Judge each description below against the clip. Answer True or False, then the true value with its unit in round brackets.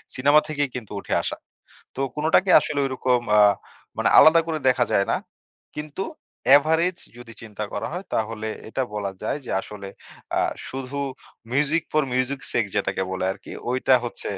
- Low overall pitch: True (130 Hz)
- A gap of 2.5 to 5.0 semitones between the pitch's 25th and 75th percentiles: False (5.5 semitones)